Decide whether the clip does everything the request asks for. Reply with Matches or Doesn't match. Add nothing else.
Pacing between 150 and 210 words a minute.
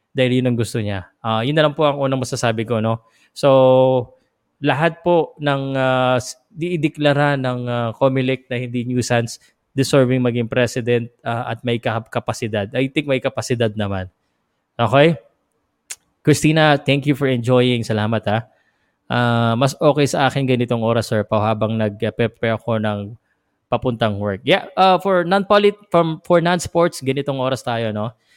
Matches